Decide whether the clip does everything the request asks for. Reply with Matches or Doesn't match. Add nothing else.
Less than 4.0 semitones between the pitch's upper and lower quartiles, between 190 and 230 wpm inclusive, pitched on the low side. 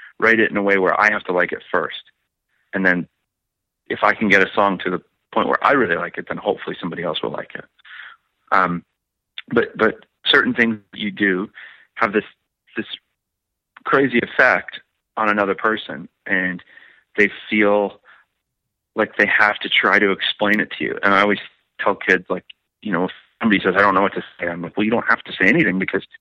Matches